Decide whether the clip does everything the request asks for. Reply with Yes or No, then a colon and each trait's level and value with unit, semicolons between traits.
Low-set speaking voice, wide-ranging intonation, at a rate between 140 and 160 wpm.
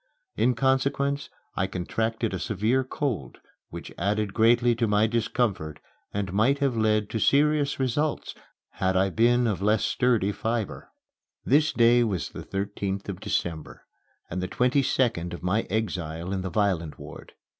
No: low, 110 Hz; average, 4.4 semitones; average, 155 wpm